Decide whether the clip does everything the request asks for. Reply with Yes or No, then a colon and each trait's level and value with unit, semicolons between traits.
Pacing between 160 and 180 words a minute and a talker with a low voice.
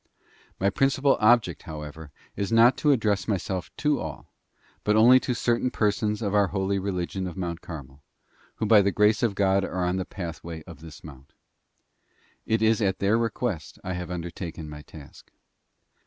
Yes: average, 170 wpm; very low, 95 Hz